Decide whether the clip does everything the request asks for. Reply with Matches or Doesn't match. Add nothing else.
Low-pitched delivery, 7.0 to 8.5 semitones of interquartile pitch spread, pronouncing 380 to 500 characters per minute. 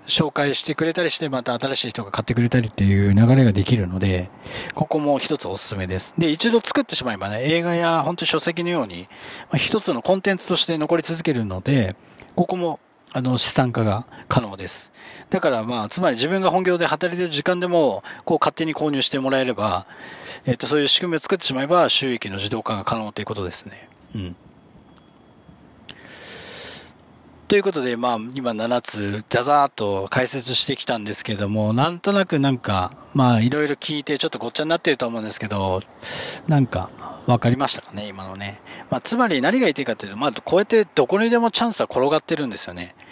Matches